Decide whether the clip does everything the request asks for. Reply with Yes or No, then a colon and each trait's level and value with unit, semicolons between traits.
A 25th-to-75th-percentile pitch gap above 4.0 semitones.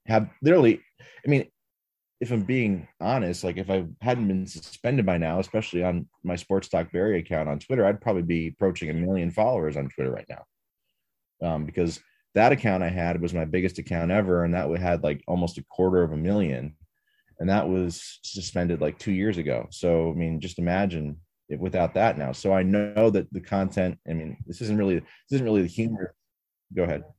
No: average, 3.3 semitones